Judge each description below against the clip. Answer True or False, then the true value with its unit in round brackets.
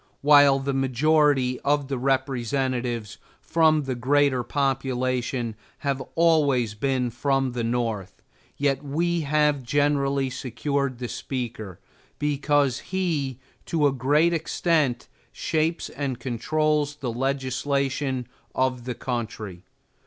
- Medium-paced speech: False (110 wpm)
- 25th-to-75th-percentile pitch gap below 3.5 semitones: True (2.7 semitones)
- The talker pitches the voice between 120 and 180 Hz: True (135 Hz)